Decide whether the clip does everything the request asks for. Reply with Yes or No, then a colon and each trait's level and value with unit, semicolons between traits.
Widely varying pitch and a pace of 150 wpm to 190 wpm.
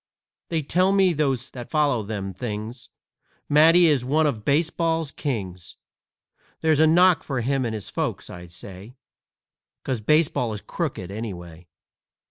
No: wide, 7.0 semitones; average, 140 wpm